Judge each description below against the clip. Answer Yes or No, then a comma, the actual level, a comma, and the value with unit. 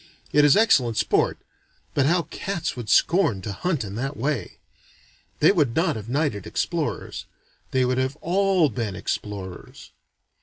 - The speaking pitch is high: No, low, 135 Hz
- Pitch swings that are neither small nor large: No, wide, 6.6 semitones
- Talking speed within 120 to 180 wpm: Yes, average, 150 wpm